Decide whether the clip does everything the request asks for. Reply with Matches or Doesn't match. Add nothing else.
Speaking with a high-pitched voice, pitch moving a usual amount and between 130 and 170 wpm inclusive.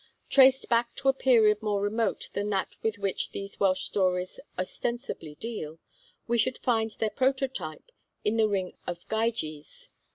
Matches